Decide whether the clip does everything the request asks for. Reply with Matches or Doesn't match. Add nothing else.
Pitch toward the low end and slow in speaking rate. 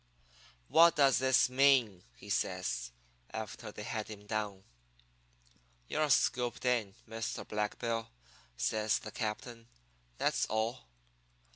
Matches